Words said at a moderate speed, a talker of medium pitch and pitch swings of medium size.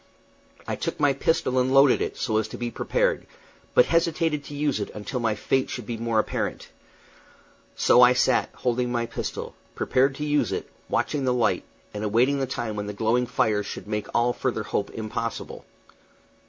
No: average, 185 wpm; low, 125 Hz; average, 3.6 semitones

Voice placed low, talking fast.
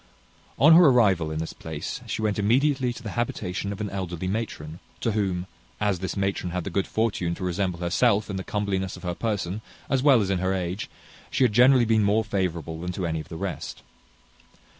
Yes: low, 100 Hz; fast, 210 wpm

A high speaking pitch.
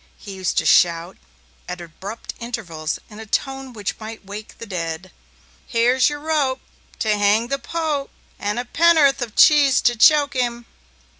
Yes: high, 235 Hz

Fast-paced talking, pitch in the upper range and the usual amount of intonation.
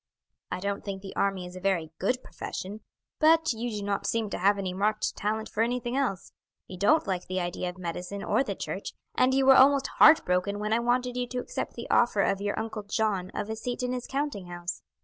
Yes: fast, 230 wpm; high, 210 Hz; average, 4.6 semitones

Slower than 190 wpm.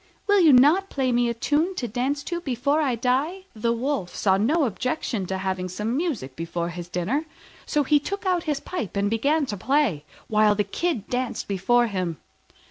No: average, 195 wpm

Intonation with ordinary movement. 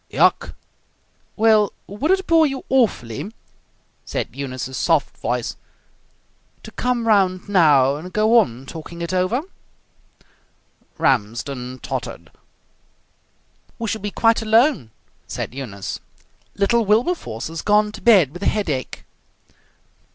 No: wide, 8.7 semitones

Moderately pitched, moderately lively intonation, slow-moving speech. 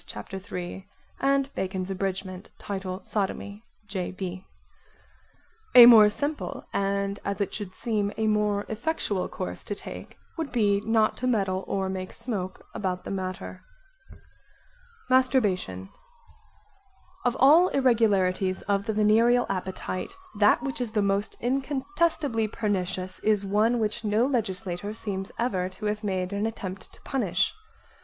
No: high, 205 Hz; average, 3.3 semitones; slow, 130 wpm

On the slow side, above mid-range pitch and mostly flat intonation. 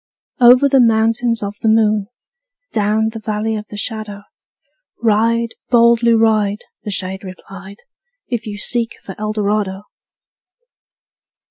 Yes: slow, 125 wpm; high, 215 Hz; narrow, 2.0 semitones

